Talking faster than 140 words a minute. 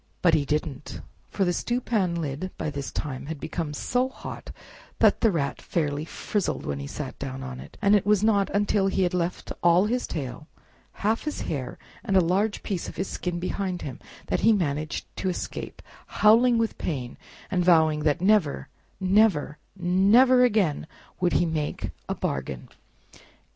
Yes: average, 175 wpm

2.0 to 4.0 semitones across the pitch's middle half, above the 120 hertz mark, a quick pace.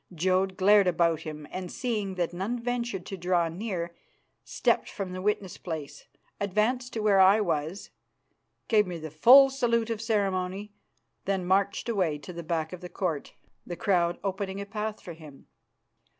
No: average, 3.5 semitones; high, 190 Hz; average, 165 wpm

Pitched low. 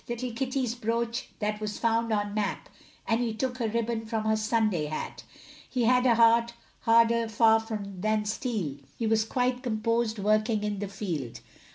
No: high, 225 Hz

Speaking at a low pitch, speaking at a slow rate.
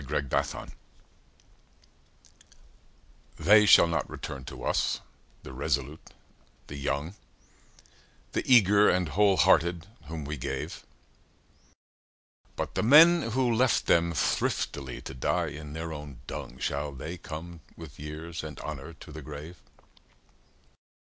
Yes: very low, 80 Hz; slow, 125 wpm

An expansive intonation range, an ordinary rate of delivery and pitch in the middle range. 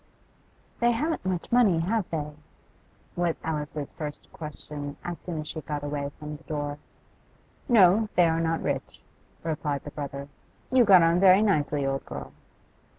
No: average, 3.9 semitones; average, 155 wpm; medium, 160 Hz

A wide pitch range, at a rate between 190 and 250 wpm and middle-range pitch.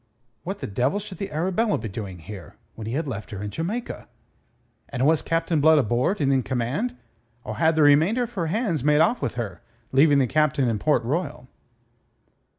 Yes: wide, 5.9 semitones; average, 195 wpm; medium, 150 Hz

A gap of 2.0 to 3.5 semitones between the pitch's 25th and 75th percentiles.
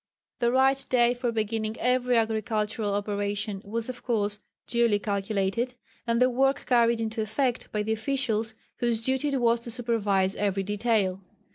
Yes: average, 2.7 semitones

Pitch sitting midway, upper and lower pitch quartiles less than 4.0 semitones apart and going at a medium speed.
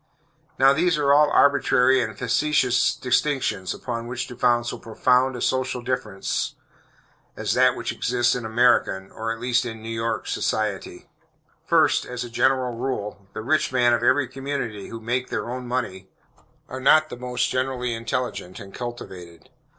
No: low, 125 Hz; narrow, 2.4 semitones; average, 165 wpm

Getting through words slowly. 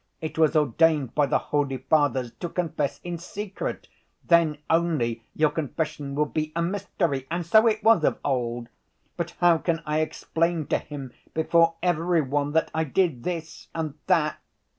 No: average, 165 wpm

